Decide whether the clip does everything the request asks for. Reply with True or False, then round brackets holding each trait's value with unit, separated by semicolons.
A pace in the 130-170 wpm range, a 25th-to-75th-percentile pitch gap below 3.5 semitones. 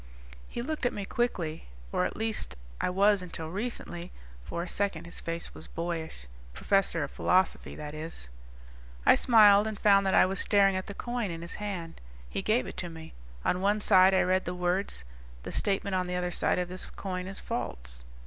False (200 wpm; 3.1 semitones)